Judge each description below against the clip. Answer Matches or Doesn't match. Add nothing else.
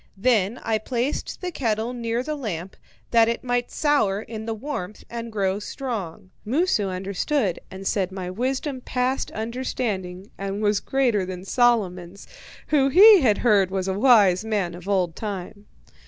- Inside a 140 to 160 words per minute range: Matches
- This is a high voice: Matches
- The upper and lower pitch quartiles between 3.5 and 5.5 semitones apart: Matches